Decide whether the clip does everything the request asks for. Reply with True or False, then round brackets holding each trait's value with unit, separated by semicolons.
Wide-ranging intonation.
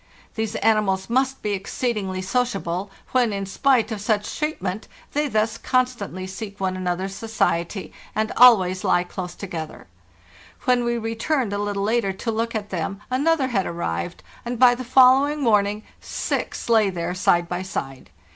False (4.4 semitones)